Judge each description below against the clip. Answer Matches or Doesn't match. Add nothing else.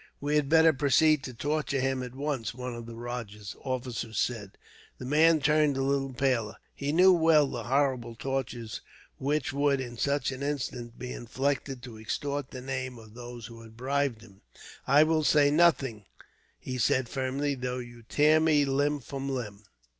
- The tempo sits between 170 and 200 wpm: Matches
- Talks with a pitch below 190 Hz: Matches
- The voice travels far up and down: Doesn't match